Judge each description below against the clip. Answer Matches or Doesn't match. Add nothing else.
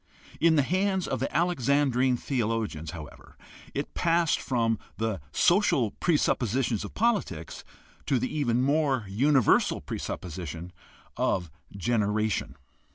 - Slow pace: Matches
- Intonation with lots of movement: Matches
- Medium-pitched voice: Doesn't match